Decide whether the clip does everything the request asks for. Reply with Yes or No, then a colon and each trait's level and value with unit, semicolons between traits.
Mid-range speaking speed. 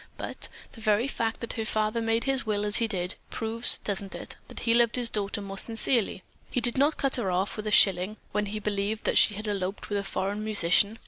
No: fast, 235 wpm